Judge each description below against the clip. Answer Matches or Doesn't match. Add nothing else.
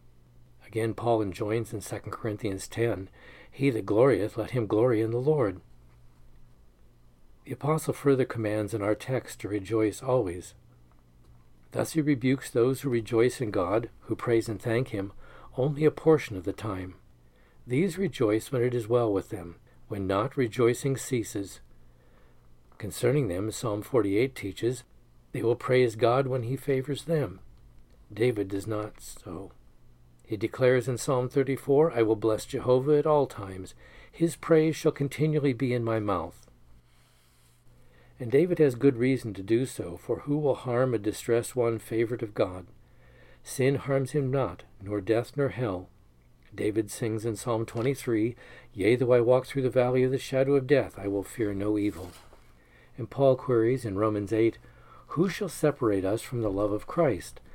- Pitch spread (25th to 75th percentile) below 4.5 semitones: Doesn't match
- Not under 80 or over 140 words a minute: Doesn't match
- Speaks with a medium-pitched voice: Doesn't match